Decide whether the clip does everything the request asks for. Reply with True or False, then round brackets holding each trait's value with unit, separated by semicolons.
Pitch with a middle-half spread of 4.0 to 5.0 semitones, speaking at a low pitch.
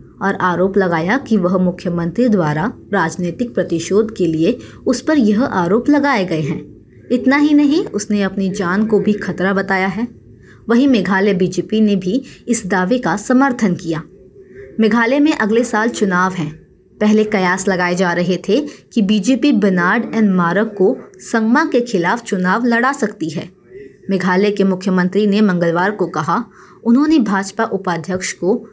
False (4.3 semitones; 205 Hz)